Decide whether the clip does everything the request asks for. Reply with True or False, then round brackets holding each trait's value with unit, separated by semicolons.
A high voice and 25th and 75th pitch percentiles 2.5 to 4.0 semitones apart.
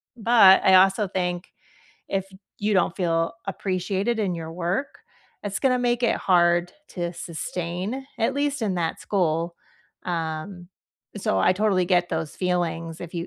False (180 Hz; 2.9 semitones)